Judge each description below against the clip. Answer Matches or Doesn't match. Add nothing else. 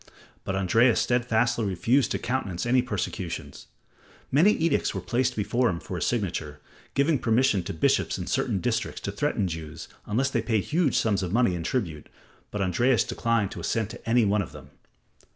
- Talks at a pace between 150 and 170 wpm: Doesn't match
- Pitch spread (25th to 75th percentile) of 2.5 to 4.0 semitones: Doesn't match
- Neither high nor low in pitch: Doesn't match